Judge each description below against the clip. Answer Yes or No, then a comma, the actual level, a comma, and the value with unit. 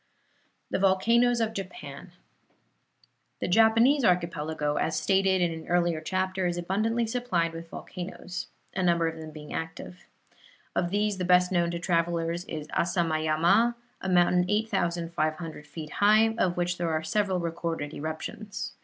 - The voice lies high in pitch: No, medium, 175 Hz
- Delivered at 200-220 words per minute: No, average, 145 wpm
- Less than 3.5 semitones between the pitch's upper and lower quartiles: Yes, average, 2.9 semitones